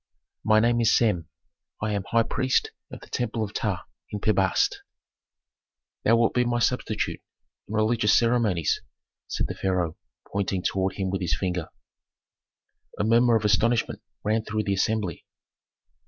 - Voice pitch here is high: No, low, 110 Hz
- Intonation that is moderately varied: Yes, average, 3.2 semitones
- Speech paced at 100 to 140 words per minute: No, average, 155 wpm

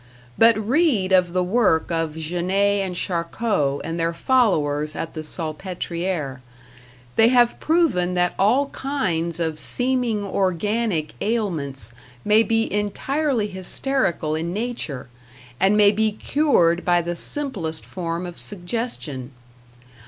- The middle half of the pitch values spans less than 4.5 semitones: No, average, 5.3 semitones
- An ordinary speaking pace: No, slow, 125 wpm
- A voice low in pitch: No, medium, 185 Hz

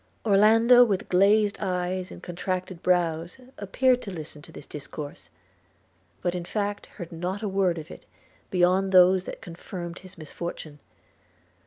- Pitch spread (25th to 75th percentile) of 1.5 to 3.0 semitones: Yes, narrow, 2.6 semitones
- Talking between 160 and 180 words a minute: No, average, 145 wpm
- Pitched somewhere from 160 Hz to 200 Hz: Yes, medium, 185 Hz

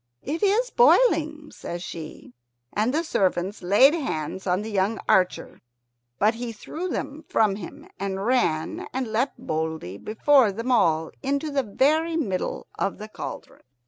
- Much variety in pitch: Yes, wide, 7.6 semitones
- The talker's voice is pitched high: Yes, high, 225 Hz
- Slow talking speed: No, average, 150 wpm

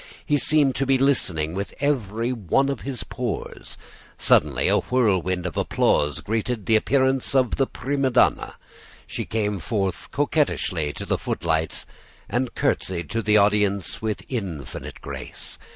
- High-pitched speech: No, low, 110 Hz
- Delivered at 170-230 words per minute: No, average, 145 wpm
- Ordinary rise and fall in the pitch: No, wide, 6.1 semitones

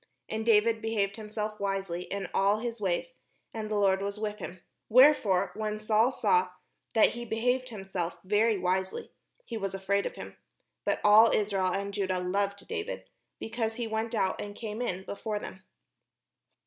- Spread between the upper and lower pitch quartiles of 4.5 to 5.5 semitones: No, narrow, 2.4 semitones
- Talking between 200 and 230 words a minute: No, average, 165 wpm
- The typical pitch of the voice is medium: No, high, 210 Hz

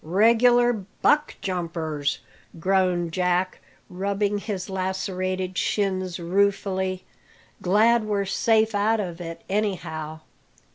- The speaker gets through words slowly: Yes, slow, 95 wpm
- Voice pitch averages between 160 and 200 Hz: Yes, high, 190 Hz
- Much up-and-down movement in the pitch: No, narrow, 2.4 semitones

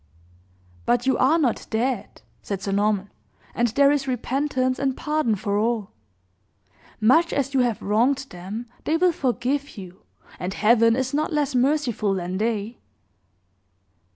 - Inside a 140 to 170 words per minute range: Yes, average, 145 wpm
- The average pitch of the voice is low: No, high, 245 Hz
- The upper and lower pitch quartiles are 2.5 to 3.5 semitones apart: No, average, 4.8 semitones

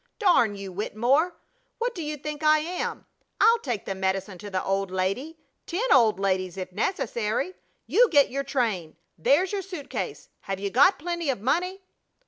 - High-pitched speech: Yes, very high, 265 Hz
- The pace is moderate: Yes, average, 175 wpm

